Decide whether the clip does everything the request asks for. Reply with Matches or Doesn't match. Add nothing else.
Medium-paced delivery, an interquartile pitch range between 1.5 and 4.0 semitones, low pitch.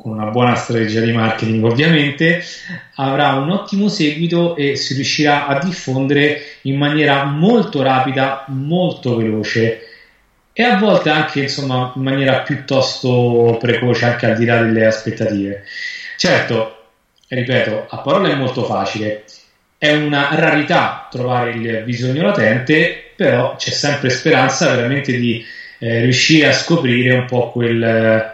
Doesn't match